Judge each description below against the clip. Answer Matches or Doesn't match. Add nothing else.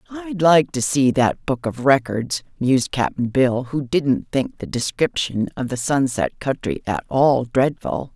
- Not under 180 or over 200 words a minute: Doesn't match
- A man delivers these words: Doesn't match